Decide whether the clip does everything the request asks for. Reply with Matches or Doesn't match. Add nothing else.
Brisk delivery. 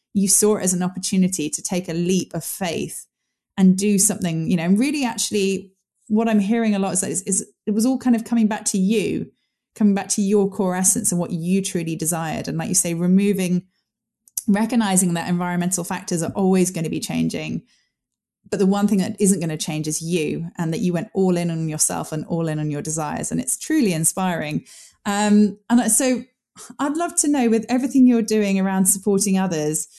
Matches